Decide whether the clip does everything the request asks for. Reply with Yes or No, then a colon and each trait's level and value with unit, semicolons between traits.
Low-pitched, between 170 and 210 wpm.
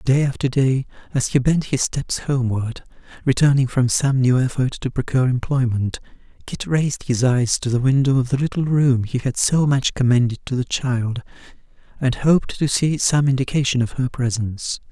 Yes: low, 130 Hz; average, 180 wpm